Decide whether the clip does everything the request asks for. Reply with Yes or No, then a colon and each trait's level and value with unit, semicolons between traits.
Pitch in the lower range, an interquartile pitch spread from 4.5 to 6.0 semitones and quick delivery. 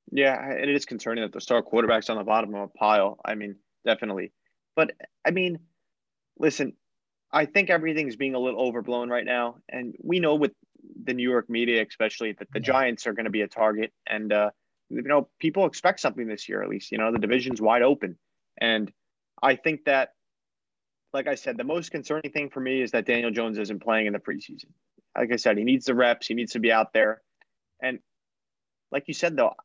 Yes: low, 125 Hz; average, 5.1 semitones; fast, 215 wpm